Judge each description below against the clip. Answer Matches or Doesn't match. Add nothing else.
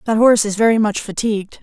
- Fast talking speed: Matches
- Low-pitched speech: Doesn't match